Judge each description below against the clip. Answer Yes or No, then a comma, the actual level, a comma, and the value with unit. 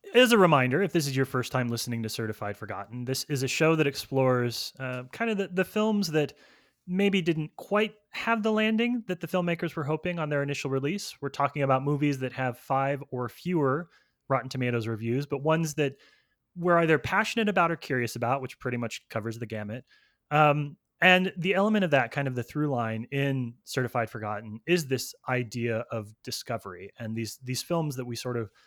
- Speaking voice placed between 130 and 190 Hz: Yes, medium, 140 Hz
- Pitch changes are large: Yes, wide, 5.8 semitones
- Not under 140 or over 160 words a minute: No, average, 200 wpm